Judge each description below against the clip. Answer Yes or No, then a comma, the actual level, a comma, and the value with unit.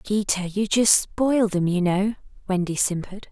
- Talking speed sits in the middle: Yes, average, 165 wpm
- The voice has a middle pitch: No, high, 195 Hz